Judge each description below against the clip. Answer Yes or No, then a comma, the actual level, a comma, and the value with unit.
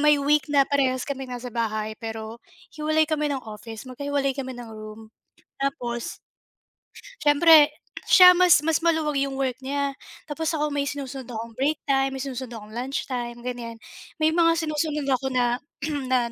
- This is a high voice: Yes, very high, 270 Hz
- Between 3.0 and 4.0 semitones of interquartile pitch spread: Yes, average, 3.7 semitones